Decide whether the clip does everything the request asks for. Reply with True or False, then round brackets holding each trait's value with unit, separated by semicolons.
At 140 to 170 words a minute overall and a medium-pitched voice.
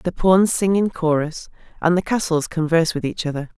False (200 wpm; 170 Hz)